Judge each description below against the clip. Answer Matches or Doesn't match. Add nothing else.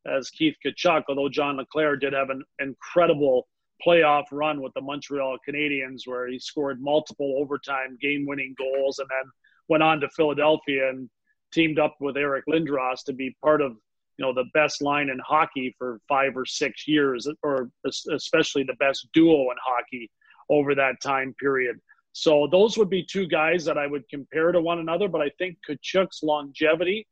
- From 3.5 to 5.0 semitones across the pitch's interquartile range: Doesn't match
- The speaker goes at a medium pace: Matches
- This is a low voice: Doesn't match